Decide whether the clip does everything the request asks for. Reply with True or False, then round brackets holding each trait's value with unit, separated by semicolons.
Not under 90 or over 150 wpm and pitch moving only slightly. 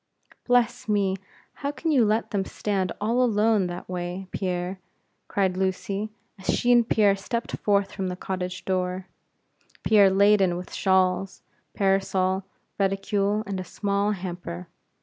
True (140 wpm; 2.2 semitones)